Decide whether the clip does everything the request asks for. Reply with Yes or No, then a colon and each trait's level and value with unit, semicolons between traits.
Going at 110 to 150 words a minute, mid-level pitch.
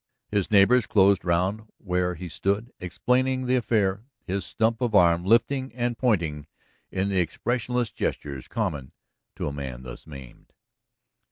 No: average, 145 wpm; low, 100 Hz